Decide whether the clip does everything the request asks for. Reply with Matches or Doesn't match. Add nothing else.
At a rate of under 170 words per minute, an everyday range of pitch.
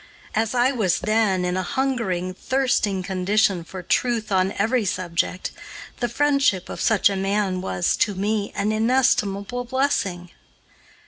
Matches